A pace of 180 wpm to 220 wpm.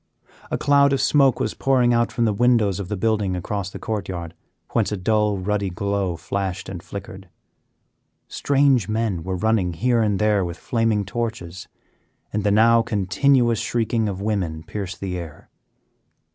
No: average, 165 wpm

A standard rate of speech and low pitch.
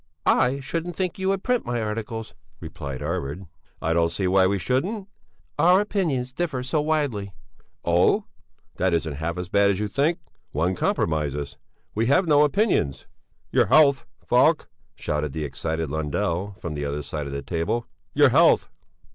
Yes: average, 165 wpm; low, 100 Hz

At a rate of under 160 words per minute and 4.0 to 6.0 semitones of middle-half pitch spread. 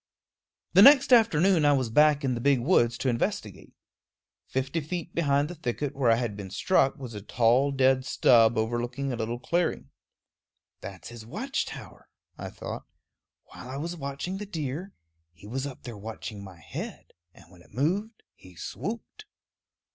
No: average, 170 wpm; wide, 5.6 semitones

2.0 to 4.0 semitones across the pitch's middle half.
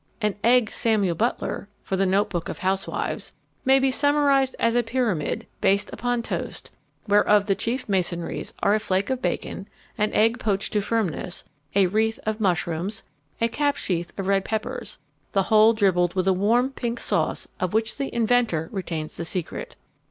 Yes: average, 3.7 semitones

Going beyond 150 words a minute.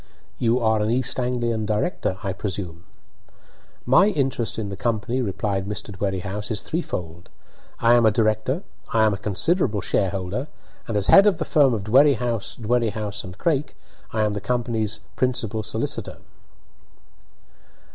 No: average, 145 wpm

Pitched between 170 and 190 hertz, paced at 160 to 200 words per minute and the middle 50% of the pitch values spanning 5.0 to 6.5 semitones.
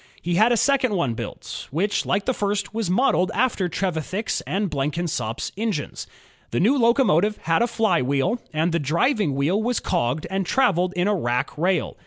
Yes: medium, 185 Hz; average, 175 wpm; wide, 5.6 semitones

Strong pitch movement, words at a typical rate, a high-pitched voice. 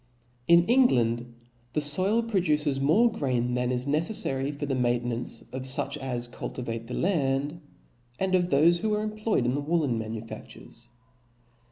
No: wide, 5.8 semitones; average, 150 wpm; medium, 140 Hz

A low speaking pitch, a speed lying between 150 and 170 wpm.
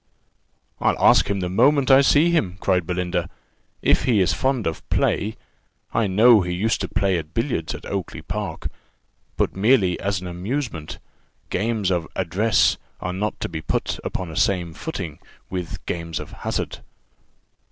Yes: very low, 95 Hz; average, 160 wpm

